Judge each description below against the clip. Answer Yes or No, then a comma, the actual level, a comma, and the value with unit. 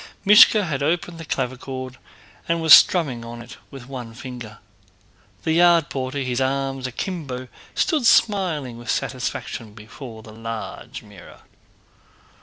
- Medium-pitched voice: No, low, 130 Hz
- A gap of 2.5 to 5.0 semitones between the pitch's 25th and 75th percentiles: No, wide, 5.4 semitones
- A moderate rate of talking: No, slow, 130 wpm